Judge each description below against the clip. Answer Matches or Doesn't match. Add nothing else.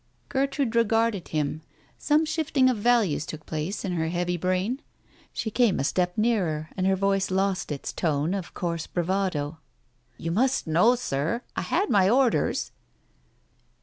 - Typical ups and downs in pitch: Doesn't match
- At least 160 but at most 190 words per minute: Doesn't match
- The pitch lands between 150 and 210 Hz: Matches